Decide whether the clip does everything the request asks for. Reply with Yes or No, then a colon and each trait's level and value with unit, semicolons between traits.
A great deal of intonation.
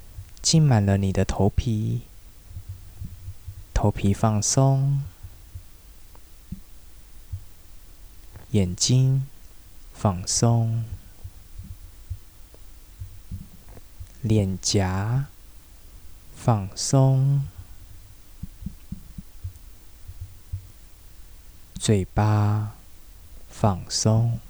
No: average, 3.2 semitones